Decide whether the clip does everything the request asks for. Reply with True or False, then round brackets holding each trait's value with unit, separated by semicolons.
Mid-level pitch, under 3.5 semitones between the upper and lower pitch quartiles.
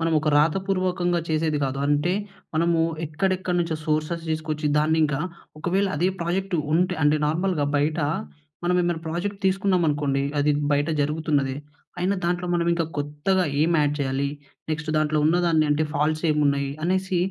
True (160 Hz; 2.9 semitones)